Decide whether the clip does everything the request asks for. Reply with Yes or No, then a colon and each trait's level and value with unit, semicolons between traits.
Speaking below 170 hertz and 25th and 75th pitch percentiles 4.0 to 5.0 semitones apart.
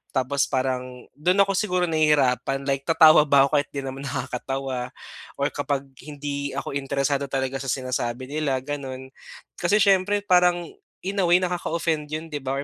No: medium, 140 Hz; average, 3.5 semitones